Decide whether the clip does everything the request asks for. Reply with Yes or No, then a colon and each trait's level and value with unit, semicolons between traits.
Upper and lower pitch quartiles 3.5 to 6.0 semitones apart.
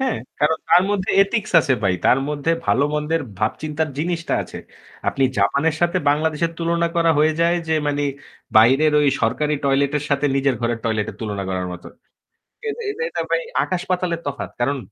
Yes: average, 4.0 semitones